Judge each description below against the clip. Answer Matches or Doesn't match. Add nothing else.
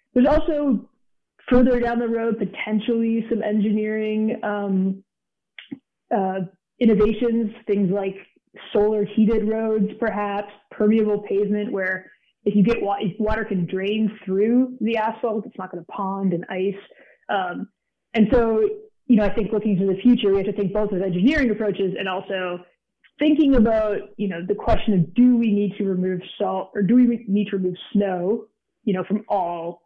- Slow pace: Doesn't match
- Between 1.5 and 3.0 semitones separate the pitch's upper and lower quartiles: Matches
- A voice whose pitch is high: Matches